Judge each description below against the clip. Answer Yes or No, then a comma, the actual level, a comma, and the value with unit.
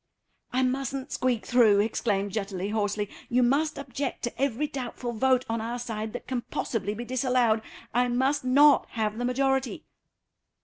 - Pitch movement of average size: Yes, average, 3.0 semitones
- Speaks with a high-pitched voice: Yes, high, 245 Hz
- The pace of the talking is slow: No, average, 160 wpm